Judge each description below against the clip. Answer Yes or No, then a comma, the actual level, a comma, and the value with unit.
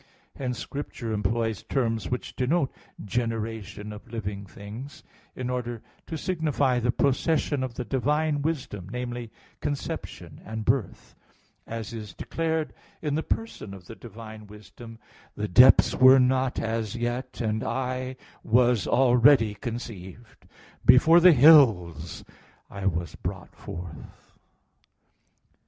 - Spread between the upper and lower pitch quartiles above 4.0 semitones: No, average, 3.7 semitones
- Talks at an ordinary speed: No, slow, 120 wpm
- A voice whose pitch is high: No, low, 120 Hz